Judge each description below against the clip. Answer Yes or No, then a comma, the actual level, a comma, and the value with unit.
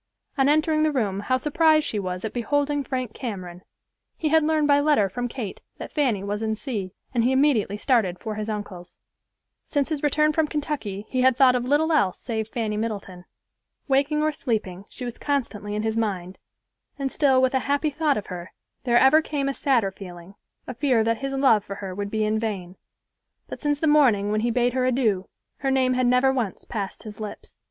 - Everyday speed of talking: No, fast, 210 wpm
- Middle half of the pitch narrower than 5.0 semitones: No, average, 5.3 semitones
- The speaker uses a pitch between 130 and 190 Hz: No, high, 245 Hz